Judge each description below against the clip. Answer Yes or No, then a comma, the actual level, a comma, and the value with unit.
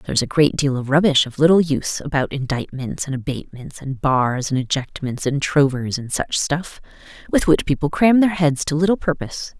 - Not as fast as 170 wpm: No, average, 200 wpm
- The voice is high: No, medium, 145 Hz